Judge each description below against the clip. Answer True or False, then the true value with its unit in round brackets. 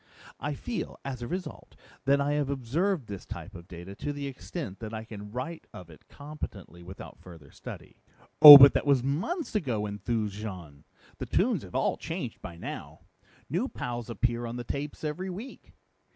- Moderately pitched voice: False (125 Hz)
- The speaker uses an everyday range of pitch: False (6.2 semitones)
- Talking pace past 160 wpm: True (180 wpm)